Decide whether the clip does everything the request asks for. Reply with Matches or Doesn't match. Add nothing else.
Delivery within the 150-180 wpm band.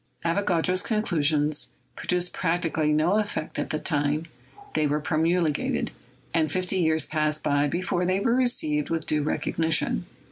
Doesn't match